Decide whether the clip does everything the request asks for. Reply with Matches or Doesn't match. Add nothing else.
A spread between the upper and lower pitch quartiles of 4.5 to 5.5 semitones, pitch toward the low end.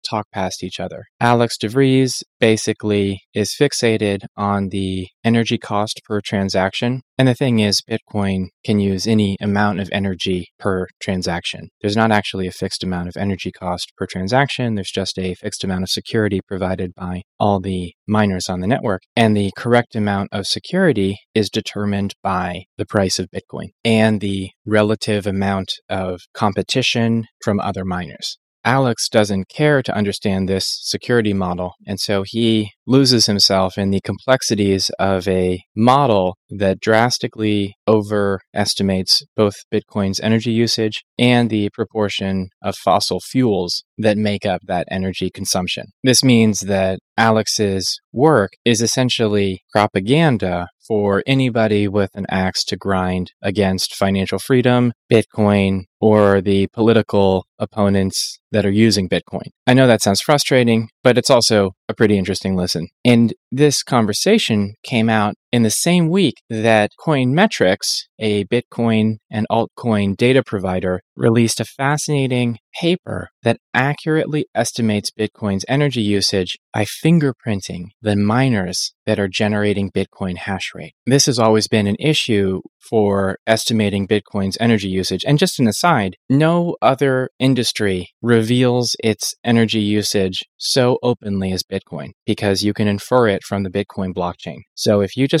Doesn't match